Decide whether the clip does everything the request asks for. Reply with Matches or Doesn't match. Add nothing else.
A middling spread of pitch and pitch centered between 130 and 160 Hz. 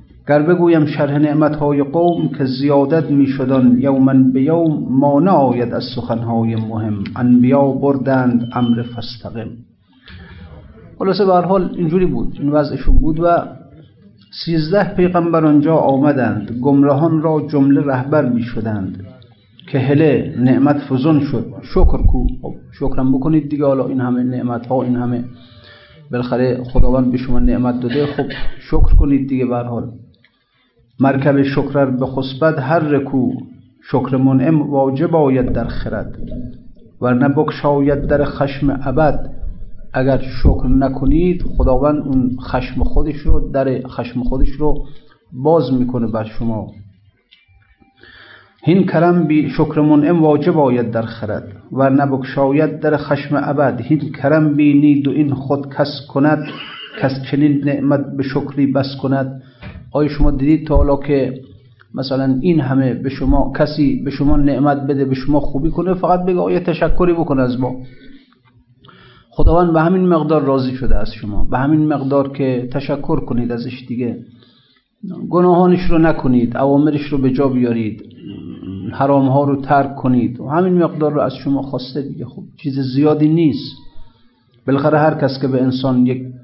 Matches